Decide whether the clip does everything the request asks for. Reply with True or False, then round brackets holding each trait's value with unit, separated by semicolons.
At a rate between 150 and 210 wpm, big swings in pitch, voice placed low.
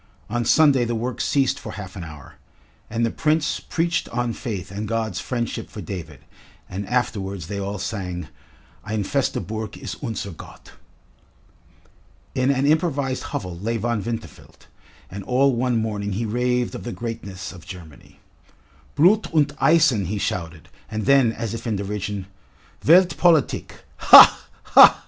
False (155 wpm; 4.5 semitones; 115 Hz)